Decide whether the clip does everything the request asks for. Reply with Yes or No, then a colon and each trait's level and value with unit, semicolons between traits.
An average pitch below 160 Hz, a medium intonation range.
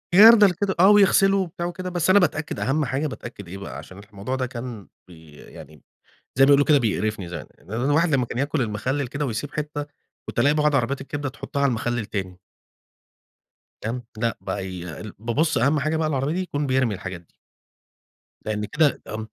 No: low, 135 Hz; wide, 6.0 semitones